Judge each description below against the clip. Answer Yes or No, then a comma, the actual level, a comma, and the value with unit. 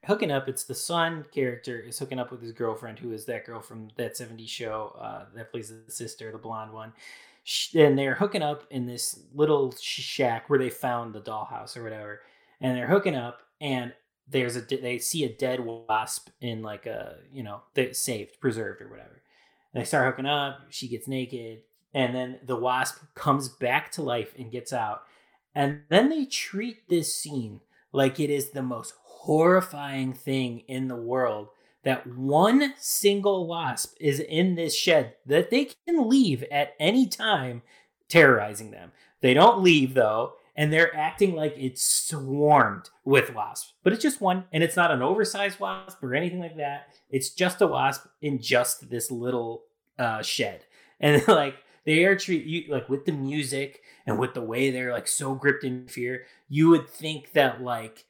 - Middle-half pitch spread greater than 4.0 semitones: Yes, average, 4.7 semitones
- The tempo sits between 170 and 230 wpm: Yes, average, 185 wpm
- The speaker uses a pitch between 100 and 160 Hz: Yes, low, 135 Hz